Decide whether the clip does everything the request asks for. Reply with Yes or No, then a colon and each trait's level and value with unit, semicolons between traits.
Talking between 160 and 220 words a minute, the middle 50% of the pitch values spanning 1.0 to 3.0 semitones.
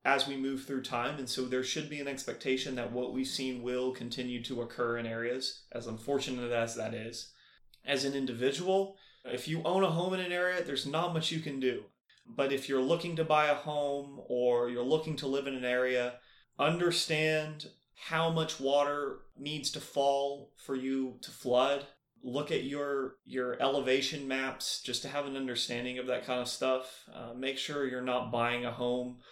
Yes: average, 195 wpm; narrow, 2.5 semitones